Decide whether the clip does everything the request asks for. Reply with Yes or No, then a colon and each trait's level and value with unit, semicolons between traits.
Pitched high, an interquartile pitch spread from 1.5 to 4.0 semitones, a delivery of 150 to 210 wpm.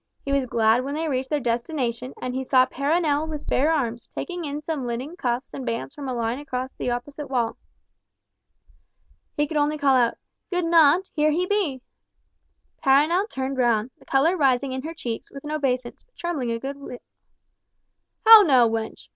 Yes: very high, 275 Hz; average, 3.6 semitones; average, 190 wpm